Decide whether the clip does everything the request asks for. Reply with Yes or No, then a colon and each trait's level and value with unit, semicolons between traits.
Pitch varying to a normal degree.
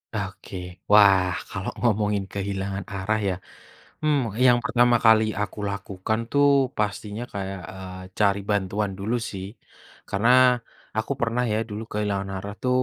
No: narrow, 2.2 semitones